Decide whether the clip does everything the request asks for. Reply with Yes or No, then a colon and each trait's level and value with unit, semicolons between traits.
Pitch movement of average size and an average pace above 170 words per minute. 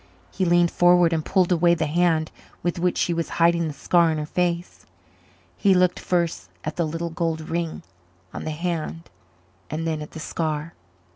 No: narrow, 1.6 semitones; average, 185 wpm